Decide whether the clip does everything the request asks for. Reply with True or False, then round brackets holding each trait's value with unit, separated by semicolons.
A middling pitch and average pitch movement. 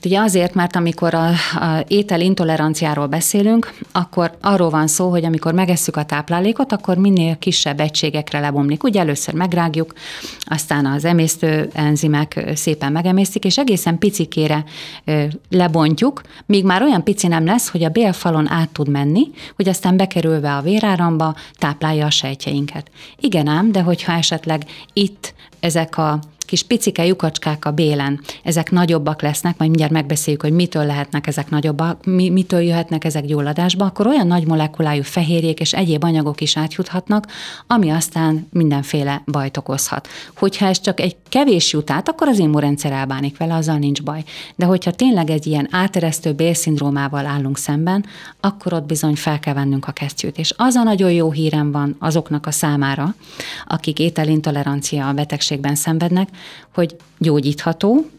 True (160 Hz; 3.2 semitones)